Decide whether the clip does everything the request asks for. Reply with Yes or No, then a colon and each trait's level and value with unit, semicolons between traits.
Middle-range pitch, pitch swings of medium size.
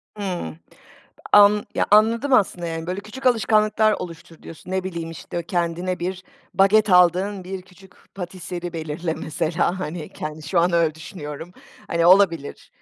Yes: medium, 180 Hz; average, 3.0 semitones